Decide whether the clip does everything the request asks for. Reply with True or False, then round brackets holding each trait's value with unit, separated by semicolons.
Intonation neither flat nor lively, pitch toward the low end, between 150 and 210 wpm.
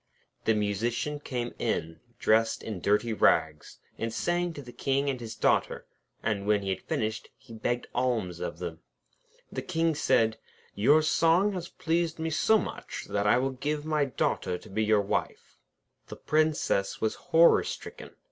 False (6.5 semitones; 120 Hz; 170 wpm)